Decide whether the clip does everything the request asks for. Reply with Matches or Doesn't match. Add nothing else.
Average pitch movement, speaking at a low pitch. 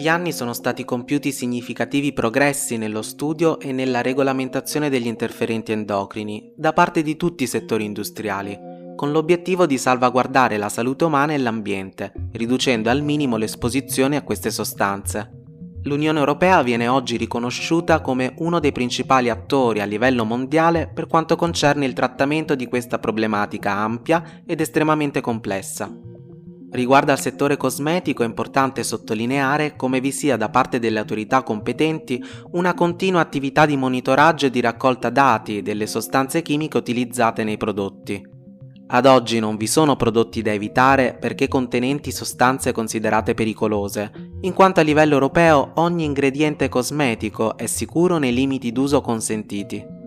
Matches